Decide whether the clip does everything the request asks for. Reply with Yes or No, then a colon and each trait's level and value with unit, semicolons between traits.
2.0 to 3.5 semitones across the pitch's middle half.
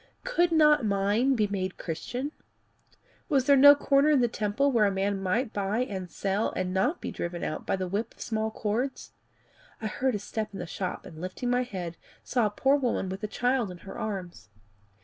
No: average, 5.1 semitones